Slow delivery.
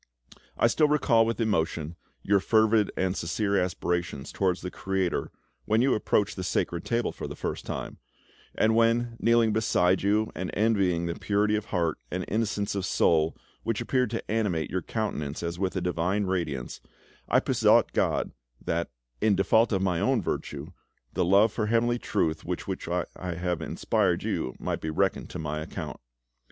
No: average, 170 wpm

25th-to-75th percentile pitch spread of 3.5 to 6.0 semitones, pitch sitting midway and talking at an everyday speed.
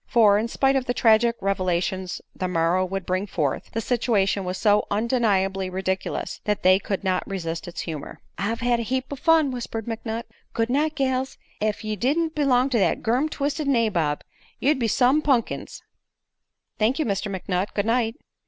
No: average, 4.9 semitones; high, 220 Hz; average, 180 wpm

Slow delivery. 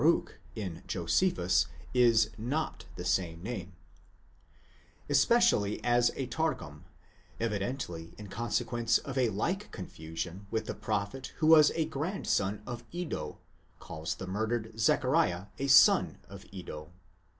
Yes: slow, 130 wpm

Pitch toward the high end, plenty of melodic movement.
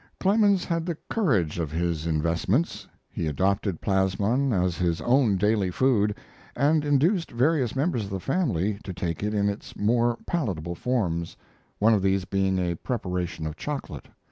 No: low, 100 Hz; wide, 6.9 semitones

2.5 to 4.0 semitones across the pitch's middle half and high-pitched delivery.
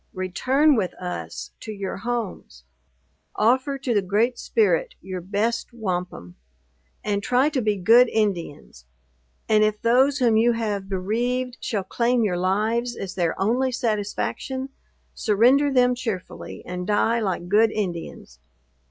No: average, 4.6 semitones; high, 215 Hz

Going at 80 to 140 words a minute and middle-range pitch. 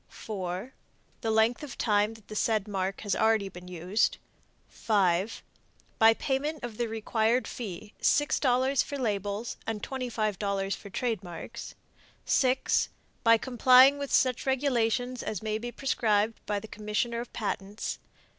No: slow, 135 wpm; high, 220 Hz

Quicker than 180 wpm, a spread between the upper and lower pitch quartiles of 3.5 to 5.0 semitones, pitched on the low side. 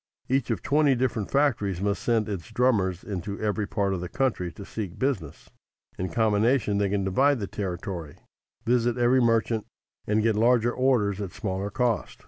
No: average, 170 wpm; average, 3.8 semitones; low, 105 Hz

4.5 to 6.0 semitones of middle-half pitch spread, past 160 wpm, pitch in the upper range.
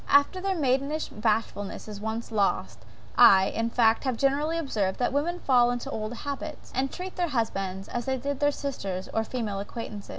Yes: average, 4.9 semitones; average, 185 wpm; high, 245 Hz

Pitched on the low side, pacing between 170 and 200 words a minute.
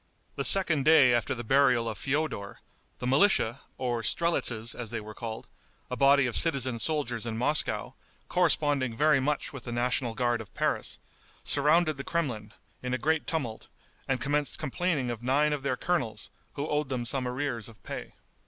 Yes: low, 130 Hz; average, 175 wpm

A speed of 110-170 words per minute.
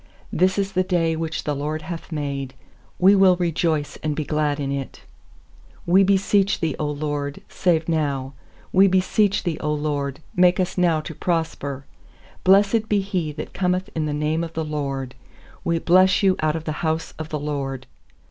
No: average, 180 wpm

